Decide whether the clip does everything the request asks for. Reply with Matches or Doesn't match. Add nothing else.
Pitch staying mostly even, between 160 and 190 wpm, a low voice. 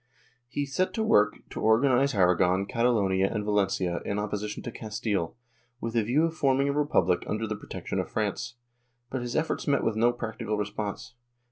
Doesn't match